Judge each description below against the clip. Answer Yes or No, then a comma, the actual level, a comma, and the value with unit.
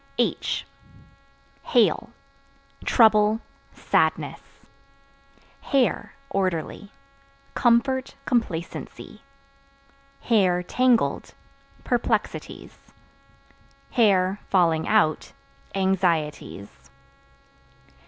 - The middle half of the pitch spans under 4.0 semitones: No, average, 4.8 semitones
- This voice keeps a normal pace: No, slow, 45 wpm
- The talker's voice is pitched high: Yes, high, 200 Hz